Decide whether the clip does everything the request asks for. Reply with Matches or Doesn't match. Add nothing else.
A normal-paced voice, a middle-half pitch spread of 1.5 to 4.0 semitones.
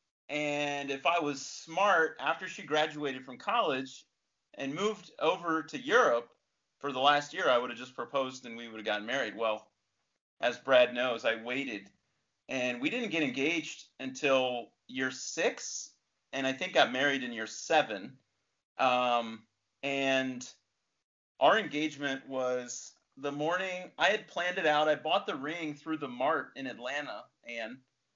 Matches